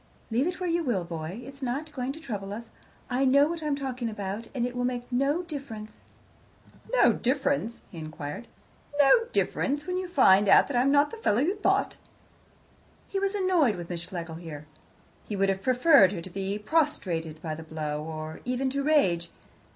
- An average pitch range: No, wide, 7.3 semitones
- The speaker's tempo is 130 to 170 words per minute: No, average, 190 wpm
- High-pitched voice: Yes, high, 245 Hz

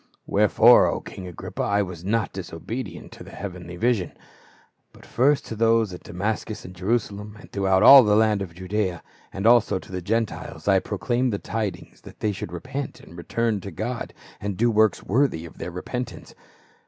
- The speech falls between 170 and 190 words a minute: Yes, average, 180 wpm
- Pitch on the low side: Yes, low, 105 Hz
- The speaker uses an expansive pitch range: No, average, 3.8 semitones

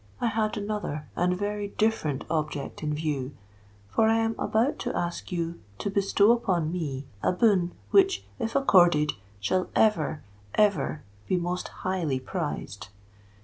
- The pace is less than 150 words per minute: Yes, average, 140 wpm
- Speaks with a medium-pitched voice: Yes, medium, 180 Hz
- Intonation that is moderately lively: No, wide, 5.8 semitones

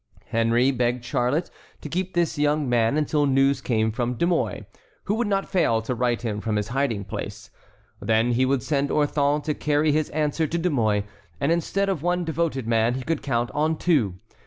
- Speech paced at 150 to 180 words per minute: No, average, 200 wpm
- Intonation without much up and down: No, average, 4.8 semitones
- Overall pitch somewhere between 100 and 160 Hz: Yes, medium, 140 Hz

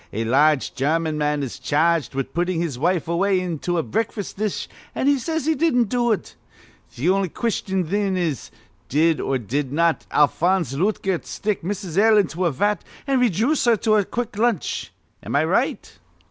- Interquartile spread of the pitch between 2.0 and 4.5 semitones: No, wide, 5.6 semitones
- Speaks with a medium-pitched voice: Yes, medium, 180 Hz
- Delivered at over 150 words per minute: Yes, average, 180 wpm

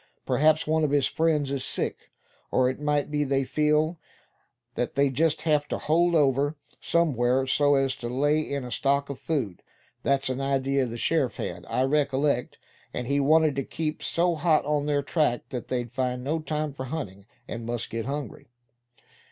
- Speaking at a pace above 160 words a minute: Yes, average, 185 wpm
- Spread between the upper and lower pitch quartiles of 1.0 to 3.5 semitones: Yes, average, 2.7 semitones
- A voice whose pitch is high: No, medium, 140 Hz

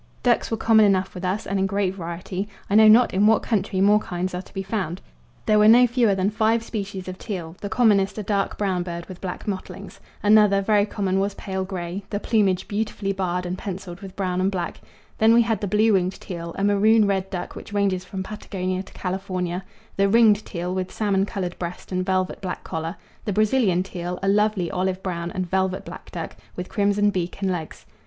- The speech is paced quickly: Yes, fast, 215 wpm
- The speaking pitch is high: Yes, high, 195 Hz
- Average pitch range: No, narrow, 2.2 semitones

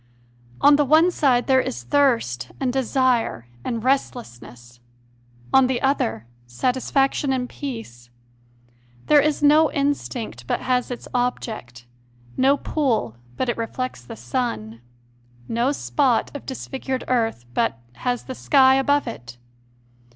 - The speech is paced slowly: Yes, slow, 130 wpm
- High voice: Yes, very high, 250 Hz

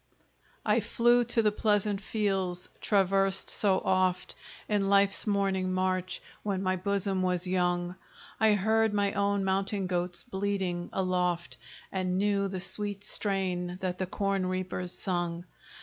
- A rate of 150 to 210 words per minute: No, slow, 135 wpm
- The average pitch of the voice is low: No, high, 190 Hz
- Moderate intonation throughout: No, narrow, 1.7 semitones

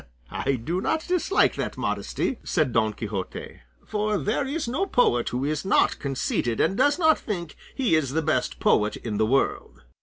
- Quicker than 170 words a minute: Yes, average, 180 wpm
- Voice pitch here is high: No, medium, 160 Hz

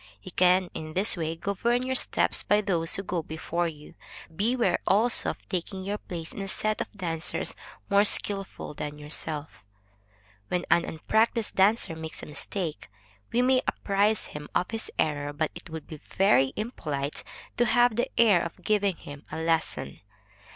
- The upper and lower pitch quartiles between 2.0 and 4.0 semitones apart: No, average, 4.7 semitones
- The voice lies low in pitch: No, medium, 180 Hz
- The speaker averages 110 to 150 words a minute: No, average, 170 wpm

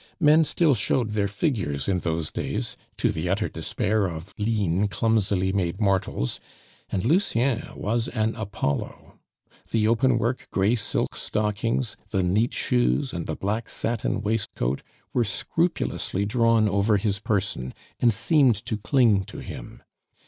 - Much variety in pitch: No, average, 3.5 semitones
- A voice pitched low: Yes, low, 105 Hz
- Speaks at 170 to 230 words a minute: No, average, 140 wpm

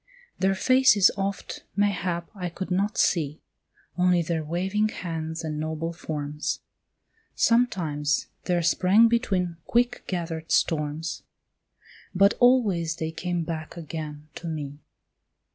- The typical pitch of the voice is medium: Yes, medium, 170 Hz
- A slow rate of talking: Yes, slow, 115 wpm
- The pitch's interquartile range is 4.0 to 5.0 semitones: No, average, 3.6 semitones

